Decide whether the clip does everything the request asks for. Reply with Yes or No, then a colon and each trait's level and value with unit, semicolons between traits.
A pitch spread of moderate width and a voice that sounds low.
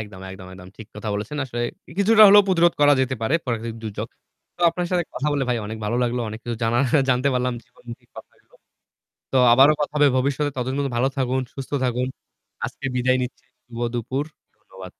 Yes: average, 3.5 semitones; low, 125 Hz